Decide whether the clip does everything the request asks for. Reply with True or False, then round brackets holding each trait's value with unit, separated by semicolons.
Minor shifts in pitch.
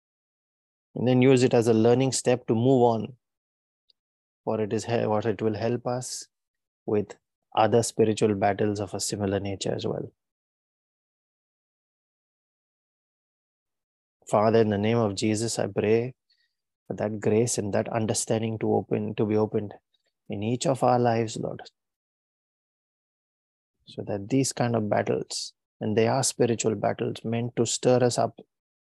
True (2.1 semitones)